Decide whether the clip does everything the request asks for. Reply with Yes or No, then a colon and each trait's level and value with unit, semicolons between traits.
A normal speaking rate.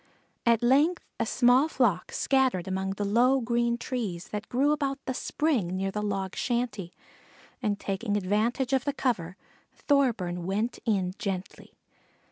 Yes: average, 145 wpm